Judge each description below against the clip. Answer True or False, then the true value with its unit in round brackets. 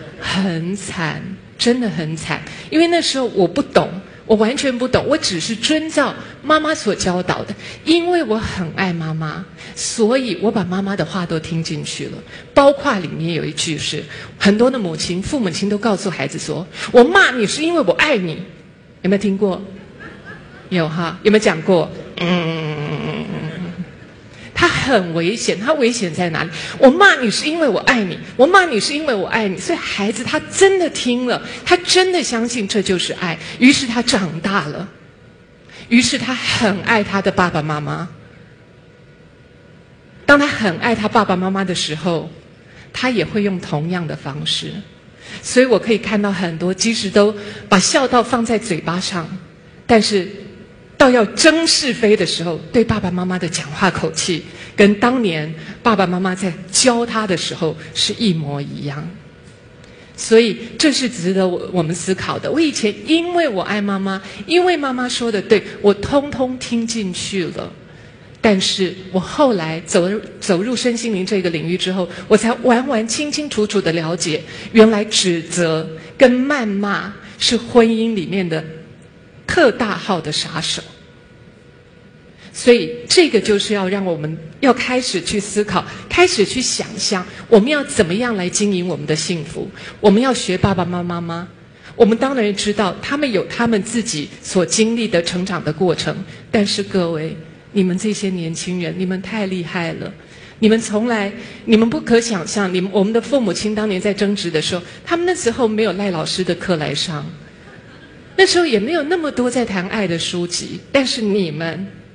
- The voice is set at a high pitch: True (200 Hz)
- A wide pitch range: False (5.0 semitones)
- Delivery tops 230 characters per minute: True (245 characters per minute)